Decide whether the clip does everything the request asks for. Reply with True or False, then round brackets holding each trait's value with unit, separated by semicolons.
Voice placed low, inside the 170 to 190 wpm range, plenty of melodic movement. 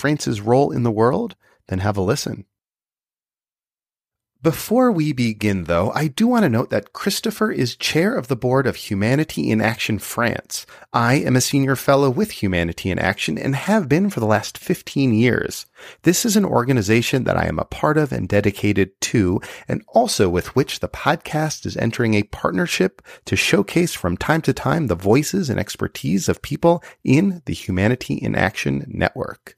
True (125 Hz; 180 wpm; 7.0 semitones)